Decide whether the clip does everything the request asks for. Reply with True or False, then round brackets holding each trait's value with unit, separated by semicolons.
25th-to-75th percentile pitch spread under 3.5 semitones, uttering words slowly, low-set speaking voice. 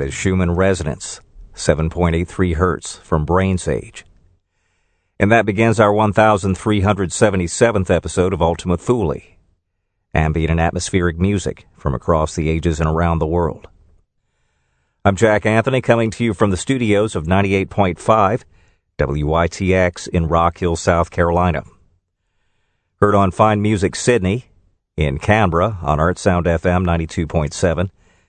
True (3.0 semitones; 120 wpm; 90 Hz)